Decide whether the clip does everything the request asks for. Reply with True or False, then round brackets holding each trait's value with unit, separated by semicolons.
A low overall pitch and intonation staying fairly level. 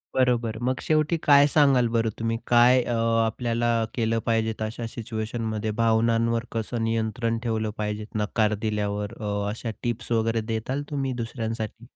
True (115 Hz; 1.5 semitones)